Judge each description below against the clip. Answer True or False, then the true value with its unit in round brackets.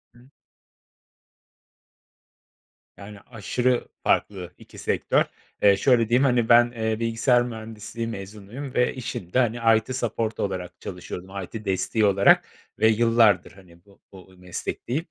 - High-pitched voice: False (110 Hz)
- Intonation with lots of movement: False (3.4 semitones)